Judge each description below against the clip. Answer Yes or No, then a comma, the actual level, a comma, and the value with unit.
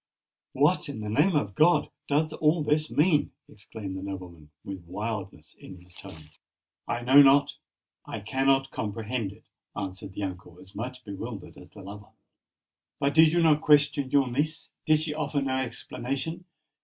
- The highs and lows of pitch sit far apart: Yes, wide, 7.0 semitones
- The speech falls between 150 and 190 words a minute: Yes, average, 160 wpm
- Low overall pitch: Yes, low, 125 Hz